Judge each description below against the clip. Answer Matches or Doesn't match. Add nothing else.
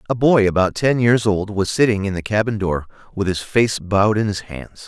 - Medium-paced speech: Doesn't match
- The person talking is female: Doesn't match